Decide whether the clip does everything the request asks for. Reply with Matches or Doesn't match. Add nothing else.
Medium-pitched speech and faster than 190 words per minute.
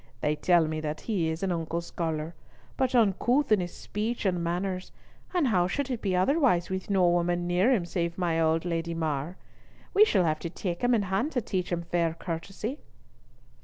Matches